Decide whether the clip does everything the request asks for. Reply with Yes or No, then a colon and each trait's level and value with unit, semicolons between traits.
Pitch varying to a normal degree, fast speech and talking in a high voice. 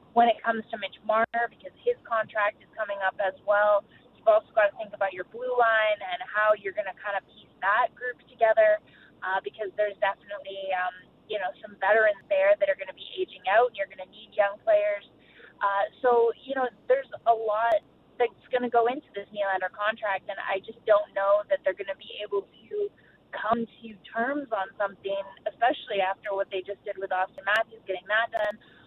Yes: average, 4.1 semitones; fast, 210 wpm; high, 215 Hz